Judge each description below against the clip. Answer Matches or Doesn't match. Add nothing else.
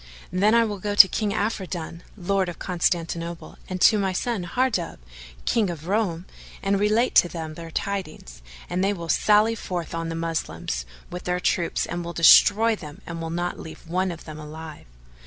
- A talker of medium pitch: Matches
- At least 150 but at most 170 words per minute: Doesn't match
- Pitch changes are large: Doesn't match